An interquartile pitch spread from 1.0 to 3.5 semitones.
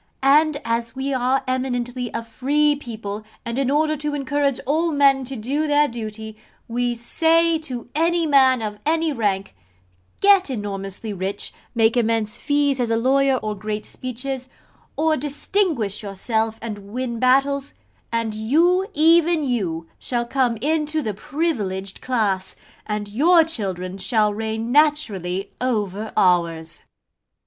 No: average, 5.3 semitones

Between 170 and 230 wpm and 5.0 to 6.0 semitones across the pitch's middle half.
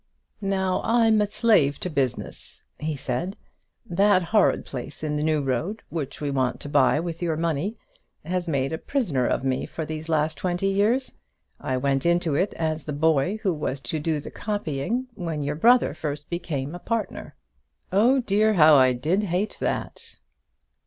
Yes: average, 175 wpm; average, 5.3 semitones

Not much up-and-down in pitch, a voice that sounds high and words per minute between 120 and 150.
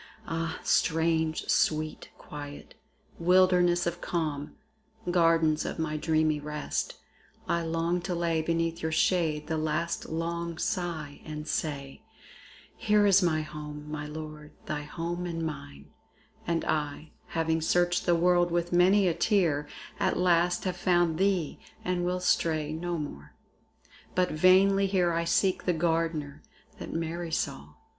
No: narrow, 2.2 semitones; medium, 165 Hz; slow, 135 wpm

